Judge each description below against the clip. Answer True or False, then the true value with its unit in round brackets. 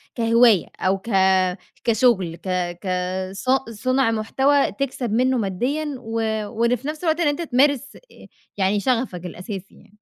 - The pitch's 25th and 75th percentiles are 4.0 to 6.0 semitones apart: True (4.9 semitones)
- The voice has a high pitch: True (240 Hz)